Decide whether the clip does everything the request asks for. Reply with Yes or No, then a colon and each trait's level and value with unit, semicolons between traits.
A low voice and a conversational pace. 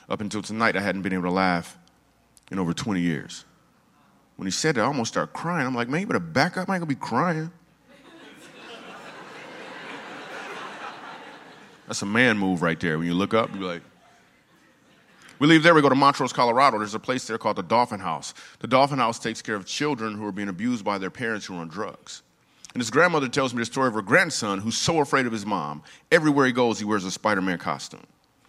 No: low, 110 Hz; fast, 220 wpm